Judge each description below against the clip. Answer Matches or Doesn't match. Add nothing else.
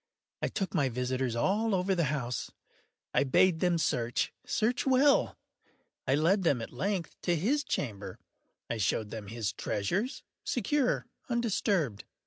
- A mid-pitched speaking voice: Matches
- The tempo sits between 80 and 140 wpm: Matches